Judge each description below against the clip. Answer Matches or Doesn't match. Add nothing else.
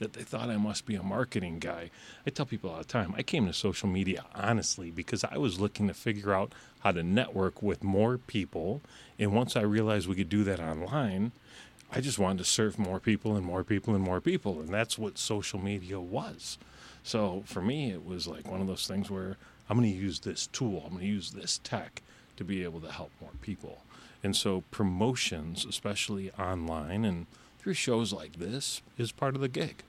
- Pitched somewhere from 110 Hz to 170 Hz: Doesn't match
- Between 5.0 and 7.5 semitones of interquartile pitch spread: Doesn't match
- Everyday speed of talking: Doesn't match